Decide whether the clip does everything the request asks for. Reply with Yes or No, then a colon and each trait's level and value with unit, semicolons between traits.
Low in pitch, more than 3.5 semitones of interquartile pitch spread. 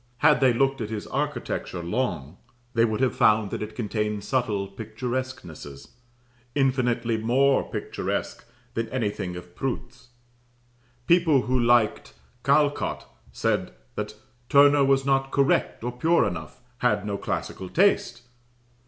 Yes: low, 120 Hz; average, 4.2 semitones